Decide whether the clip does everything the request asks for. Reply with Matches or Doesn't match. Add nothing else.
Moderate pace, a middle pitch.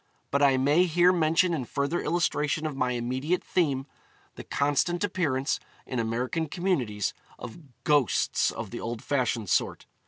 Matches